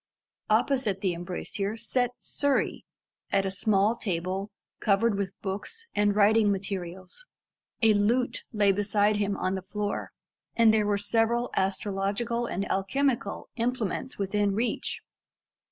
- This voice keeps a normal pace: No, slow, 125 wpm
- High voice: Yes, high, 205 Hz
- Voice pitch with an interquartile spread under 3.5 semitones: Yes, average, 2.9 semitones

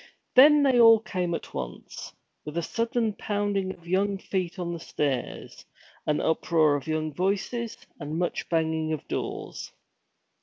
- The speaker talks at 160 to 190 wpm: No, average, 150 wpm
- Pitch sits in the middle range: Yes, medium, 175 Hz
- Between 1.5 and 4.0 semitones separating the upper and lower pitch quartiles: No, average, 4.5 semitones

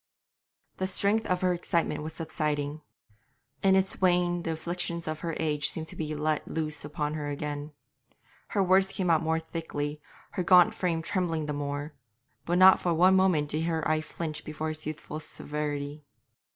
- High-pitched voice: No, medium, 160 Hz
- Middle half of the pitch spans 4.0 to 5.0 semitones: No, average, 2.7 semitones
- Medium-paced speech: Yes, average, 170 wpm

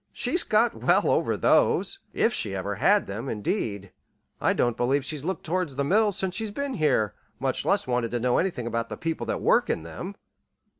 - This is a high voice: No, medium, 145 Hz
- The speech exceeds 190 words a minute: Yes, average, 200 wpm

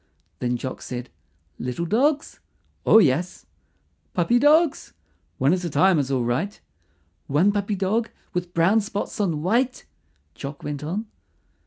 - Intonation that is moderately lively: No, wide, 7.0 semitones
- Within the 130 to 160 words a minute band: Yes, average, 140 wpm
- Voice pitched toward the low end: No, medium, 180 Hz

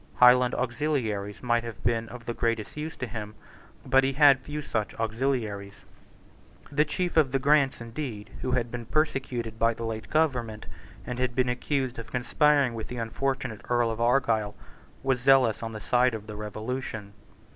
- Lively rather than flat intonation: No, average, 3.0 semitones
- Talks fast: No, average, 175 wpm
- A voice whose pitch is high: No, low, 120 Hz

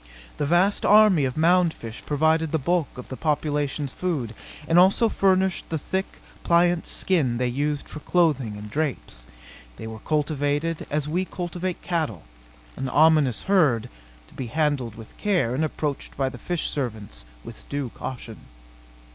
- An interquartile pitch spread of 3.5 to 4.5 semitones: No, average, 5.1 semitones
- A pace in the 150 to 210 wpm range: Yes, average, 155 wpm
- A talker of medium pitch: Yes, medium, 150 Hz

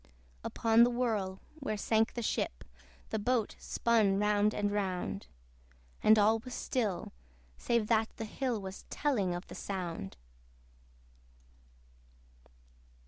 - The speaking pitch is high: Yes, high, 215 Hz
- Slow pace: Yes, slow, 120 wpm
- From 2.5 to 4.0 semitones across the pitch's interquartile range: Yes, average, 2.9 semitones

